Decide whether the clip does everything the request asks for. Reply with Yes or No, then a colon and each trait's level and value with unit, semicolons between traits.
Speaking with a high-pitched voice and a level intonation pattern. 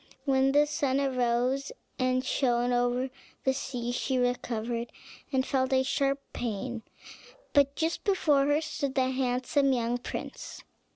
Yes: very high, 260 Hz; narrow, 2.1 semitones